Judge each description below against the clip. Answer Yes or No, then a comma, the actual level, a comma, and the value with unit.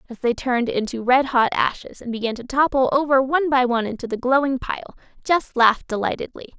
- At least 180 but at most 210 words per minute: Yes, average, 200 wpm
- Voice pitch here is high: Yes, very high, 250 Hz